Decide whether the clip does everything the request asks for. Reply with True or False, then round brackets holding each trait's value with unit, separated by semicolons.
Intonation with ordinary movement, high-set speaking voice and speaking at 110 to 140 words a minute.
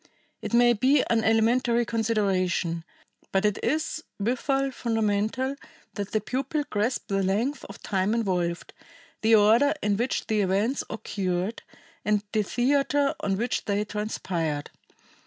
True (3.6 semitones; 220 Hz; 135 wpm)